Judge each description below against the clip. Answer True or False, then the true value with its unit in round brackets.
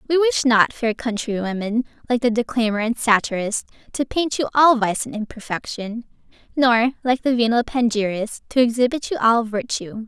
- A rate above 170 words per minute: False (160 wpm)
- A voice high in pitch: True (235 Hz)